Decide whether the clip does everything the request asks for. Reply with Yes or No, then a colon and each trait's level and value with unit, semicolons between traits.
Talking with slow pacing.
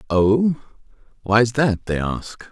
Yes: slow, 120 wpm